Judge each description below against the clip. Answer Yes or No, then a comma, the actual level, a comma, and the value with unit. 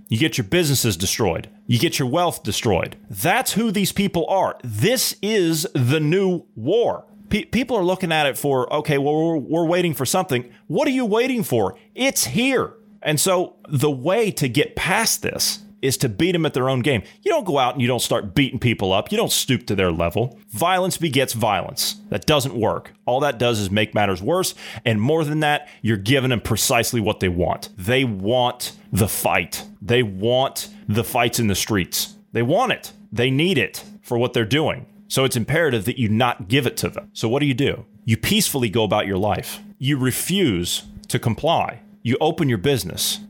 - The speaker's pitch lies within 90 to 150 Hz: Yes, medium, 140 Hz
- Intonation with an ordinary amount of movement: No, wide, 7.6 semitones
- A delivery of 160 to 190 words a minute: No, fast, 205 wpm